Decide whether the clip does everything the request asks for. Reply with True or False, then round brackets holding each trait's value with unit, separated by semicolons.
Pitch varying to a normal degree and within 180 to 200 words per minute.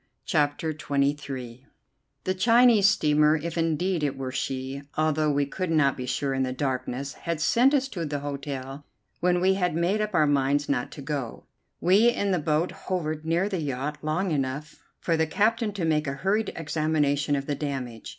True (4.2 semitones; 185 wpm)